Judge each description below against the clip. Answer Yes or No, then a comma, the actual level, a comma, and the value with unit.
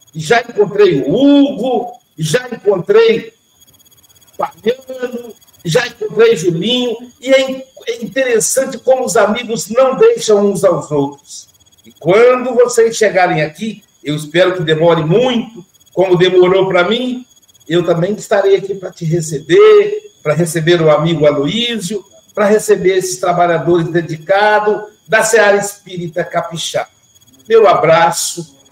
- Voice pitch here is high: Yes, high, 205 Hz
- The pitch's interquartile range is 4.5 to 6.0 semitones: Yes, wide, 5.5 semitones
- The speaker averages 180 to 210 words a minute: No, average, 125 wpm